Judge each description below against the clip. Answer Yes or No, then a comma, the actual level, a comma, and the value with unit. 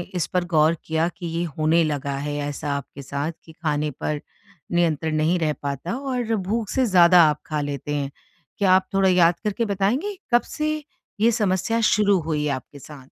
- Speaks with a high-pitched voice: No, medium, 170 Hz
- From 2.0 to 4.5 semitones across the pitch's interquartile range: No, average, 5.3 semitones